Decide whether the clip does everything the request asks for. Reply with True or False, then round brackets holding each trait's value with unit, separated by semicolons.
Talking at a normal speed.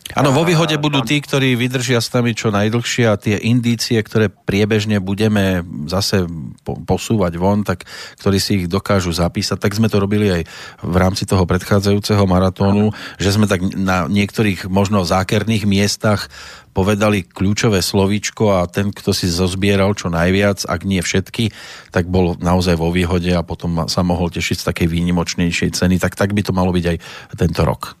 False (170 wpm)